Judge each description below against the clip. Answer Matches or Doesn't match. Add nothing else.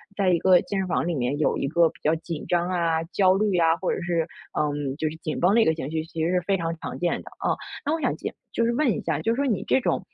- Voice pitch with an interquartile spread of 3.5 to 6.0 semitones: Doesn't match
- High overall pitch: Doesn't match